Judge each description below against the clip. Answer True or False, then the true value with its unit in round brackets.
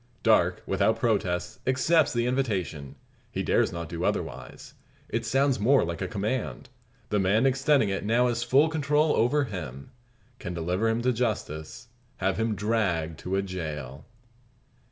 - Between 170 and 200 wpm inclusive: False (155 wpm)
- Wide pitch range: True (6.5 semitones)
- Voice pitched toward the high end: False (110 Hz)